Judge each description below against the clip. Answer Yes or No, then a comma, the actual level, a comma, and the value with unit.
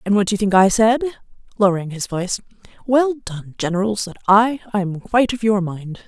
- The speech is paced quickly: No, average, 190 wpm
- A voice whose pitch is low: No, high, 205 Hz